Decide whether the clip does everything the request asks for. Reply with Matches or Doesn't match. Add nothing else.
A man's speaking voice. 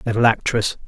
Matches